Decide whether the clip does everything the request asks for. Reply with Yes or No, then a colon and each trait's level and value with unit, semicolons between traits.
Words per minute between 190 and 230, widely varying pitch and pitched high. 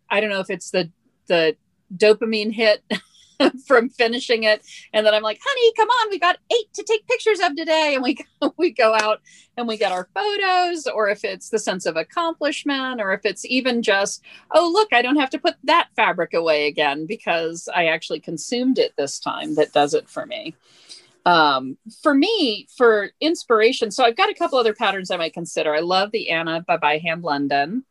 Yes: average, 200 wpm; wide, 8.6 semitones; high, 225 Hz